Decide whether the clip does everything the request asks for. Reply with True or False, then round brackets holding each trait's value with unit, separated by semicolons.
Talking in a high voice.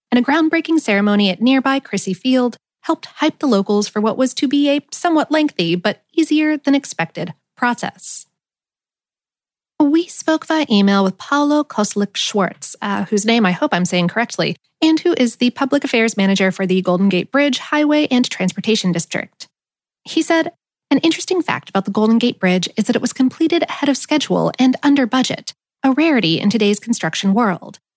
True (245 Hz)